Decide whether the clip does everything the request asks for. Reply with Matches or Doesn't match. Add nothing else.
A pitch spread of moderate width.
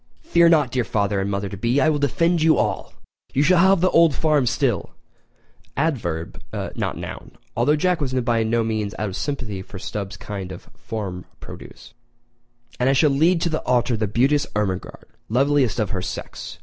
Doesn't match